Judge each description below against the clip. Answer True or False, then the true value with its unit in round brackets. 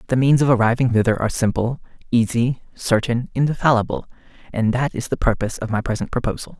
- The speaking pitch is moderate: False (120 Hz)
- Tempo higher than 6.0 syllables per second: True (6.2 syllables/s)